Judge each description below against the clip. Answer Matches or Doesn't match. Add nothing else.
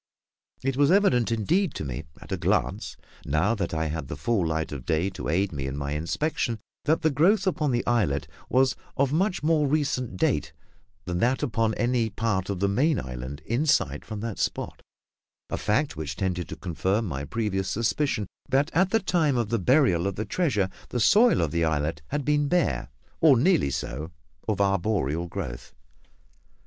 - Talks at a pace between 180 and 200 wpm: Matches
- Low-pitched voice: Matches